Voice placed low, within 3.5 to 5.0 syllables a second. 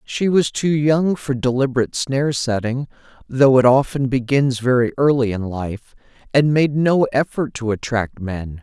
Yes: low, 130 Hz; 4.6 syllables/s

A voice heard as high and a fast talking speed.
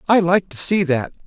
No: medium, 170 Hz; fast, 240 wpm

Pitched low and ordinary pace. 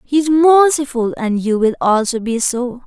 No: very high, 255 Hz; average, 190 wpm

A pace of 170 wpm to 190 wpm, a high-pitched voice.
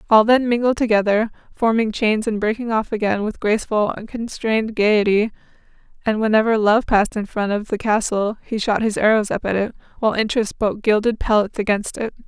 Yes: average, 180 wpm; high, 215 Hz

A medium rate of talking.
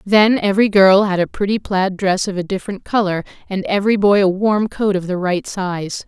No: fast, 215 wpm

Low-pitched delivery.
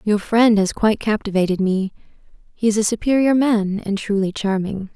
No: high, 210 Hz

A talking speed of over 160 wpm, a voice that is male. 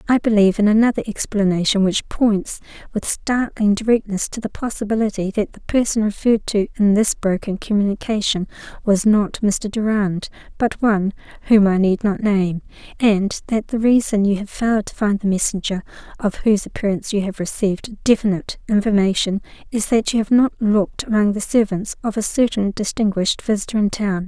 No: average, 170 wpm; female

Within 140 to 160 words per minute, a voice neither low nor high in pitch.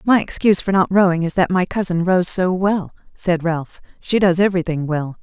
No: fast, 205 wpm; medium, 180 Hz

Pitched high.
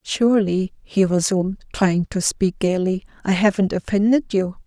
Yes: high, 195 Hz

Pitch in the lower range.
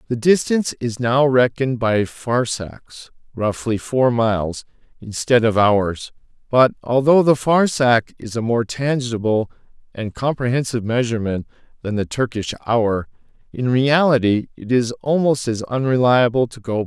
Yes: low, 120 Hz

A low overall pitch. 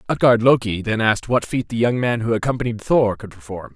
Yes: low, 115 Hz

